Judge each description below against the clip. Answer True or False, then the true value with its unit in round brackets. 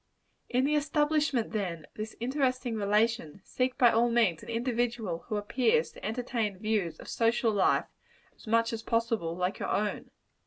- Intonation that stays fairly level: False (3.1 semitones)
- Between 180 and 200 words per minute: False (165 wpm)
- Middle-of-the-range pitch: False (230 Hz)